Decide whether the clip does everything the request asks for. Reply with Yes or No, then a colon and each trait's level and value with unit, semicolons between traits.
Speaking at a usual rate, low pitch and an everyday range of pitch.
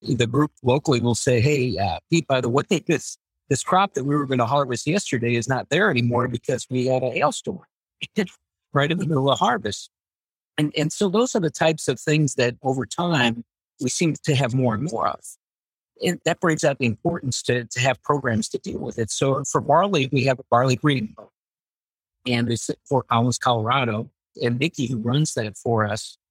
No: fast, 210 wpm; low, 130 Hz; average, 4.1 semitones